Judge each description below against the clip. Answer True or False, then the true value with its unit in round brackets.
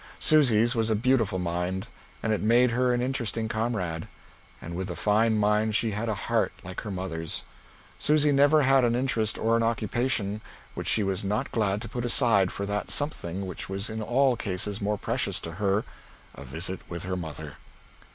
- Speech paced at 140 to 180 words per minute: False (190 wpm)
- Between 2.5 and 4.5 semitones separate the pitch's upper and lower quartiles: True (3.9 semitones)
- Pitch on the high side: False (105 Hz)